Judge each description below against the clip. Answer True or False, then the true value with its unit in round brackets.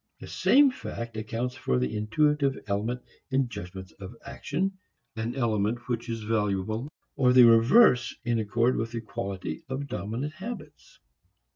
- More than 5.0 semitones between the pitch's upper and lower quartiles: False (4.0 semitones)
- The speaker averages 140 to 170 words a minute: True (145 wpm)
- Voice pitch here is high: False (115 Hz)